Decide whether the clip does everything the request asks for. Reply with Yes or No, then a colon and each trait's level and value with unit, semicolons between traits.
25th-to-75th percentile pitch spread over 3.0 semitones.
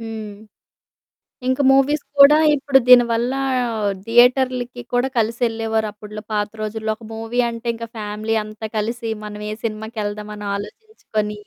No: narrow, 2.5 semitones